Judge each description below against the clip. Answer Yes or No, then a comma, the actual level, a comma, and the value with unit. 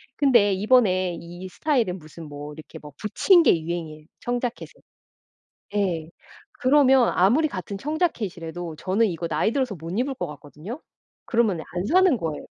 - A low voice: No, high, 190 Hz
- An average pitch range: No, wide, 7.0 semitones